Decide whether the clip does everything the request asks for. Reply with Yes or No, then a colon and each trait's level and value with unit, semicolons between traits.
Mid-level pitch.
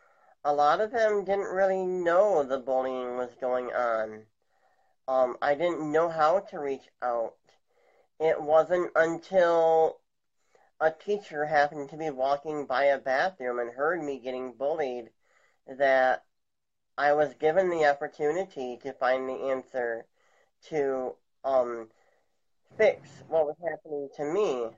Yes: medium, 145 Hz